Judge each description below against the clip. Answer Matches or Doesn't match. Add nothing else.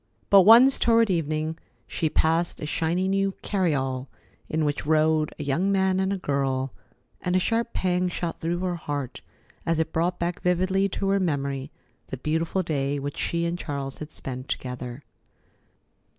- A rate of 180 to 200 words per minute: Doesn't match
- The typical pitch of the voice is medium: Matches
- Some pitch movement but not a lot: Matches